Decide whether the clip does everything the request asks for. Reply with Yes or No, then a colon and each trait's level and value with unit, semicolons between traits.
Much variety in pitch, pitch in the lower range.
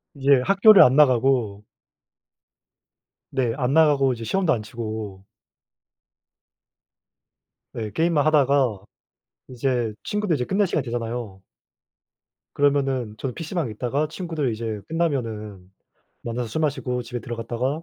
No: average, 4.7 semitones; low, 125 Hz